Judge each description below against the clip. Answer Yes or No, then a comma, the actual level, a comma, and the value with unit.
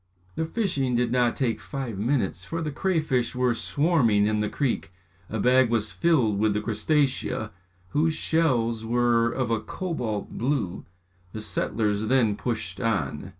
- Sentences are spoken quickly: No, average, 150 wpm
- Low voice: Yes, low, 120 Hz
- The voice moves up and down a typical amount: Yes, average, 4.3 semitones